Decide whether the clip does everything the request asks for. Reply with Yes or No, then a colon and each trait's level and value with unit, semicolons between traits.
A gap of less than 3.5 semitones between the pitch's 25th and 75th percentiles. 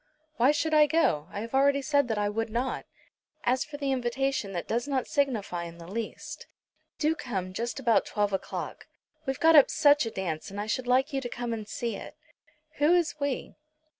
No: average, 5.2 semitones